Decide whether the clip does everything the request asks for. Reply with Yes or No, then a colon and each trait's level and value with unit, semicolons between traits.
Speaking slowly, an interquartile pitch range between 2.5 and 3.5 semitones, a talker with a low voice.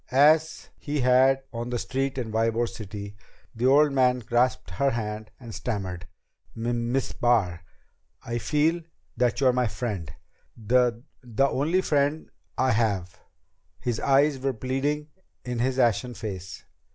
No: average, 145 wpm; average, 3.2 semitones; low, 125 Hz